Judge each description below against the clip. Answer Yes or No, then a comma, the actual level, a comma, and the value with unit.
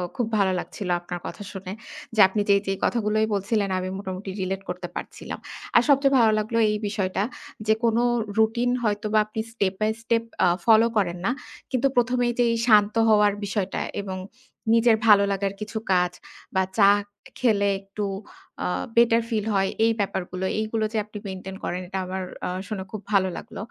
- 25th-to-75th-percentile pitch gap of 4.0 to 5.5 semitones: No, average, 2.7 semitones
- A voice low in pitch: No, high, 210 Hz